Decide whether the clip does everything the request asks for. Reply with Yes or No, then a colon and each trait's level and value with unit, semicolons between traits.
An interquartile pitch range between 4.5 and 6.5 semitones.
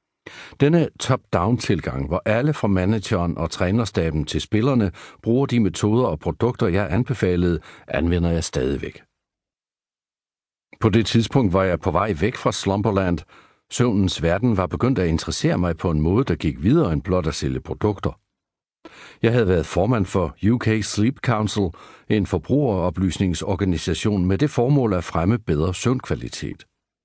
Yes: average, 4.8 semitones